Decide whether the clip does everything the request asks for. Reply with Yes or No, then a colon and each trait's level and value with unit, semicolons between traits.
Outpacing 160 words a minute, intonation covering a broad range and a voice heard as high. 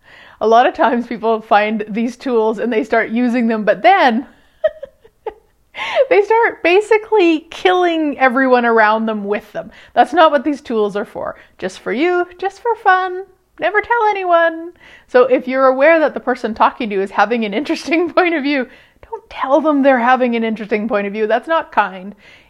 Yes: average, 185 wpm; wide, 7.1 semitones; very high, 265 Hz